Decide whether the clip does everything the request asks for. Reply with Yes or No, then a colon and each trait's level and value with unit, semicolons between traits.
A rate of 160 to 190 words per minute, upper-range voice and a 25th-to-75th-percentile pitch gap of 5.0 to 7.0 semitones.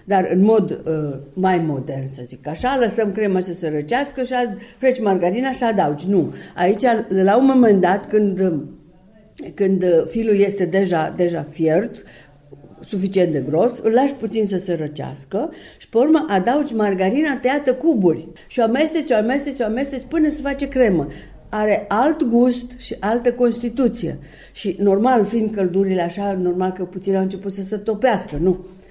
Yes: average, 165 wpm; high, 200 Hz; average, 5.3 semitones